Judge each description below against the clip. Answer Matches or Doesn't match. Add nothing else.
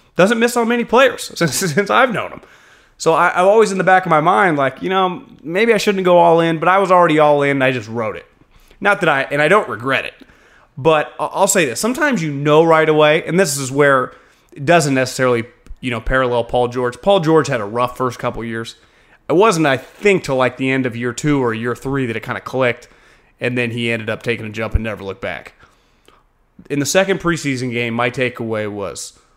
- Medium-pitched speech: Matches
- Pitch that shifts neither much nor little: Doesn't match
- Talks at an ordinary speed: Doesn't match